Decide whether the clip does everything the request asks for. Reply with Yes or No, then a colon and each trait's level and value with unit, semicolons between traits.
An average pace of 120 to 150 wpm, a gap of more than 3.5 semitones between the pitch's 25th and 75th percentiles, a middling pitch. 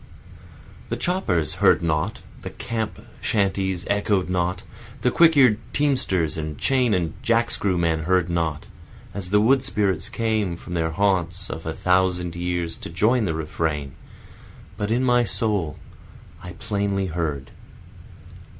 No: average, 140 wpm; average, 4.7 semitones; very low, 95 Hz